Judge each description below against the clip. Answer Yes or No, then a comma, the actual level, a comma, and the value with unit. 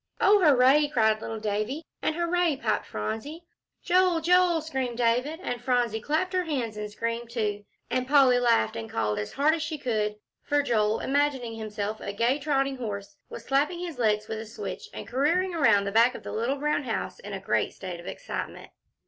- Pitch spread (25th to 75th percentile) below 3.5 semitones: No, wide, 5.6 semitones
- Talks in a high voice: Yes, very high, 250 Hz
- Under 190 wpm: No, average, 195 wpm